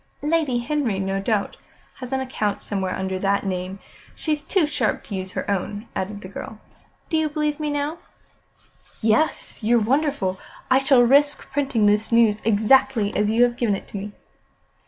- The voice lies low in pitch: No, high, 225 Hz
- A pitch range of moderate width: No, wide, 5.9 semitones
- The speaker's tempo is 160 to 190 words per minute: Yes, average, 175 wpm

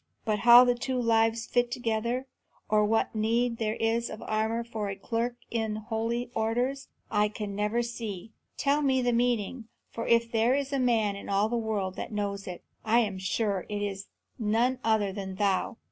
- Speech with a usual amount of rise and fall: No, narrow, 2.3 semitones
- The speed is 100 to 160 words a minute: No, average, 190 wpm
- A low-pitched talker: No, high, 225 Hz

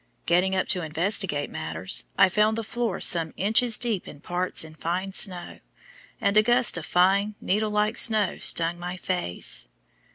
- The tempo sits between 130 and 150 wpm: No, average, 165 wpm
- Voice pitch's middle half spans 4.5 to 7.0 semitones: No, average, 3.7 semitones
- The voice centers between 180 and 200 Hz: Yes, medium, 185 Hz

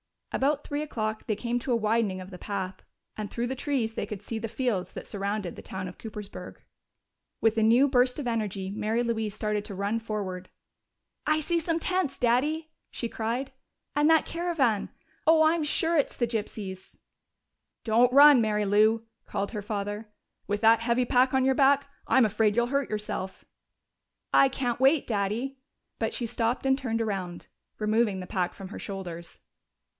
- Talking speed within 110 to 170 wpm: No, average, 180 wpm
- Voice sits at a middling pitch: No, high, 225 Hz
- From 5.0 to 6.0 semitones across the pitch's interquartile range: No, average, 4.3 semitones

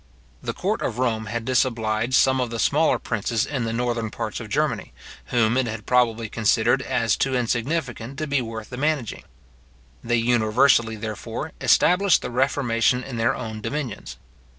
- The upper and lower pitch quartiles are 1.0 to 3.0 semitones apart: Yes, narrow, 2.5 semitones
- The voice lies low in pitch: Yes, low, 120 Hz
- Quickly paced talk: No, average, 165 wpm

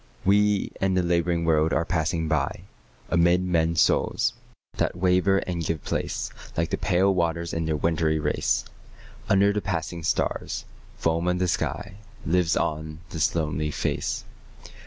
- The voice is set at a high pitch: No, very low, 85 Hz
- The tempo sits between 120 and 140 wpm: No, average, 150 wpm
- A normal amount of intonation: No, narrow, 2.1 semitones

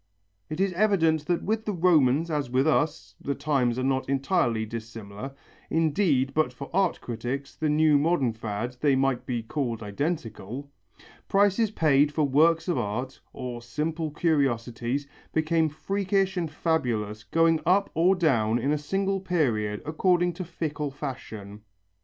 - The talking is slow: No, average, 150 wpm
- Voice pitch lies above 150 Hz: No, medium, 145 Hz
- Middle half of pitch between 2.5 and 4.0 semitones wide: No, average, 5.2 semitones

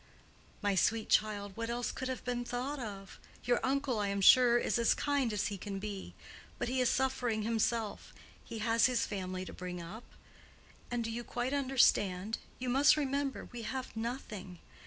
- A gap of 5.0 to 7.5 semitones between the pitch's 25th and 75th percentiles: No, average, 3.7 semitones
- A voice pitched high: Yes, high, 230 Hz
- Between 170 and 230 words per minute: Yes, average, 180 wpm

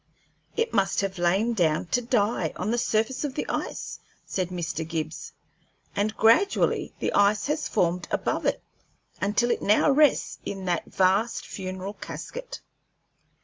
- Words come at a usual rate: Yes, average, 145 wpm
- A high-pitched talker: Yes, high, 205 Hz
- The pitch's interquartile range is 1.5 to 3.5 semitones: No, average, 4.6 semitones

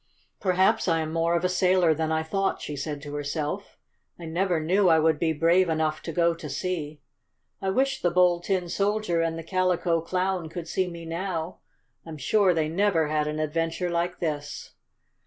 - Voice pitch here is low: No, medium, 170 Hz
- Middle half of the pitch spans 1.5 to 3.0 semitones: Yes, narrow, 2.5 semitones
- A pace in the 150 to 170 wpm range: No, average, 195 wpm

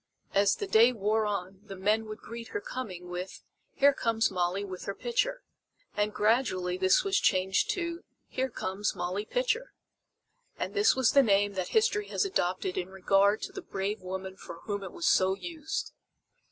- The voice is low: No, high, 205 Hz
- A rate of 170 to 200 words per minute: Yes, average, 180 wpm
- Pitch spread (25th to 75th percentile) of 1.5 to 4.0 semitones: No, wide, 5.4 semitones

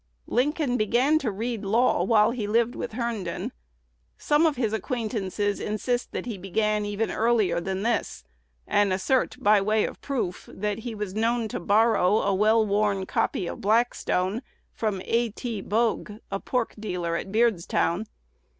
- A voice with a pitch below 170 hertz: No, high, 215 Hz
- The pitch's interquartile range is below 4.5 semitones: Yes, average, 3.0 semitones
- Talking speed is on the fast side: No, average, 160 wpm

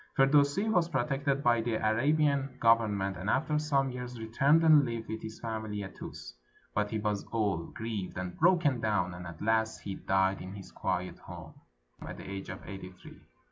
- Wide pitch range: Yes, wide, 5.7 semitones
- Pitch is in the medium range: No, low, 110 Hz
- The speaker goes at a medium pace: Yes, average, 180 wpm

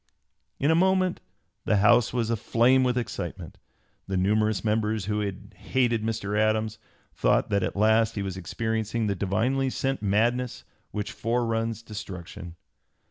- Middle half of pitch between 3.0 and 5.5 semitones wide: No, narrow, 2.5 semitones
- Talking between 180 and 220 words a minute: No, slow, 135 wpm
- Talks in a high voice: No, low, 110 Hz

